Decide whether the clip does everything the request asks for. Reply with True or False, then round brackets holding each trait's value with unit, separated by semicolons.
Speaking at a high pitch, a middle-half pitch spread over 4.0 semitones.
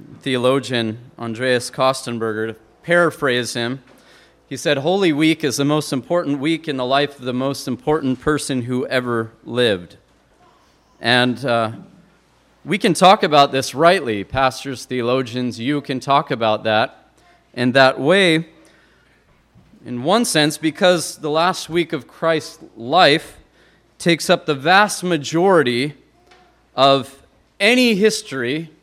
False (140 Hz; 4.6 semitones)